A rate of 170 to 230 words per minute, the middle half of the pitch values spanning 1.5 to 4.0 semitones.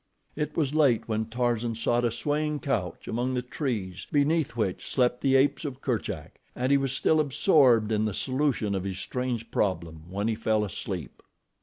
No: average, 180 wpm; average, 4.4 semitones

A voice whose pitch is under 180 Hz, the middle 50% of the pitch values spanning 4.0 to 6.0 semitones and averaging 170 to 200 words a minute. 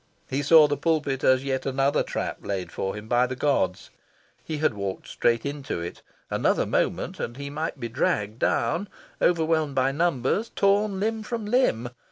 Yes: medium, 140 Hz; average, 5.2 semitones; average, 175 wpm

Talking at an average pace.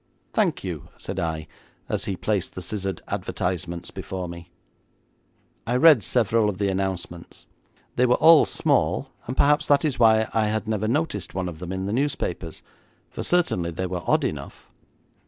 Yes: average, 170 wpm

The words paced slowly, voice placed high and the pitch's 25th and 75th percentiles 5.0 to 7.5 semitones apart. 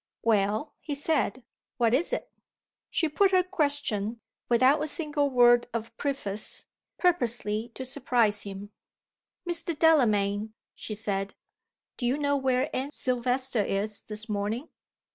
Yes: slow, 130 wpm; high, 245 Hz; average, 5.3 semitones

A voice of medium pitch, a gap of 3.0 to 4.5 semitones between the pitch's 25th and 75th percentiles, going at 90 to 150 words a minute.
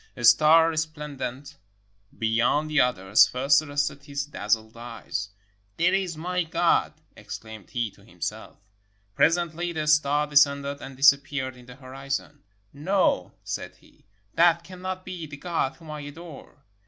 Yes: medium, 145 Hz; average, 3.8 semitones; average, 140 wpm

